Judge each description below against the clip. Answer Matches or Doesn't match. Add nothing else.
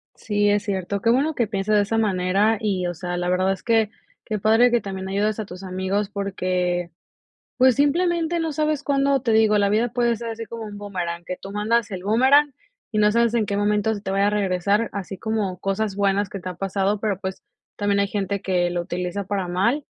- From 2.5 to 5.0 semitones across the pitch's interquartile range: Matches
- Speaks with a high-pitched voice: Matches